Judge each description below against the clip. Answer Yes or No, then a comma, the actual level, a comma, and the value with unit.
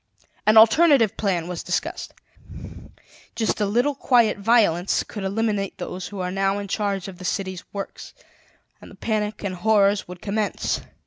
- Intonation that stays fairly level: Yes, narrow, 2.3 semitones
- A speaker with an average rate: Yes, average, 155 wpm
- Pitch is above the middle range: Yes, high, 200 Hz